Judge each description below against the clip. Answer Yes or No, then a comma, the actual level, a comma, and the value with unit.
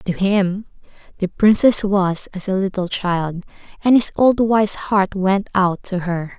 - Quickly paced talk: No, average, 170 wpm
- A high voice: Yes, high, 195 Hz